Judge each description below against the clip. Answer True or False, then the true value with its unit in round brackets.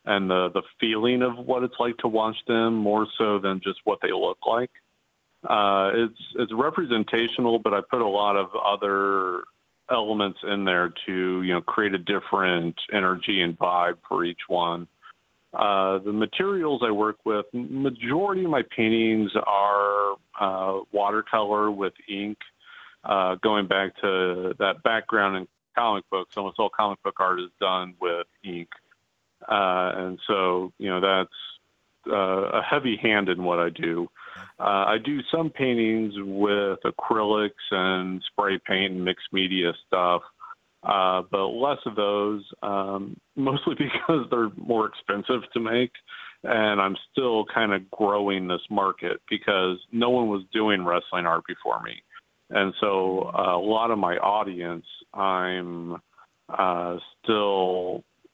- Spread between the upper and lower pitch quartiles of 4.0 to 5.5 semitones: False (3.0 semitones)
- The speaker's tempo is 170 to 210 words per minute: False (150 wpm)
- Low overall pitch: True (100 Hz)